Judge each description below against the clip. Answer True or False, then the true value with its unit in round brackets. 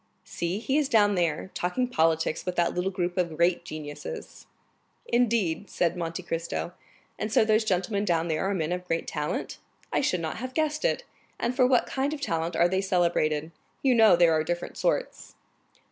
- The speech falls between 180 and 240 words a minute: True (190 wpm)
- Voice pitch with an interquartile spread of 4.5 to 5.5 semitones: True (5.1 semitones)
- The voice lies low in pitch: False (180 Hz)